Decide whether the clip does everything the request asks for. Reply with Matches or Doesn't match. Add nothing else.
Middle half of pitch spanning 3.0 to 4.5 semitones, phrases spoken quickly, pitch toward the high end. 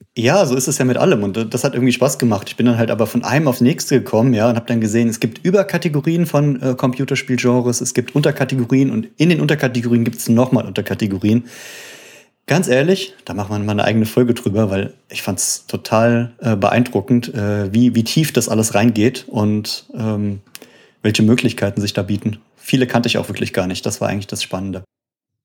Doesn't match